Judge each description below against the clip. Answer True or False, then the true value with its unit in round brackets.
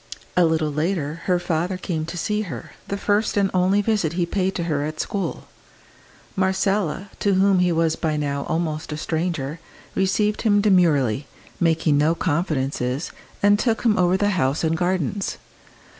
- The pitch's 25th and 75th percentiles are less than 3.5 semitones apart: False (3.8 semitones)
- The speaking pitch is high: False (175 Hz)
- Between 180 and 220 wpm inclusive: False (165 wpm)